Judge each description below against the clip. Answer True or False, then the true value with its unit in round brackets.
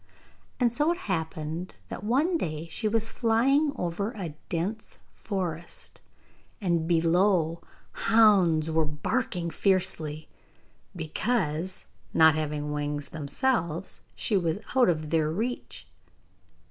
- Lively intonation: True (5.8 semitones)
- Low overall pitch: False (175 Hz)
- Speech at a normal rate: False (110 wpm)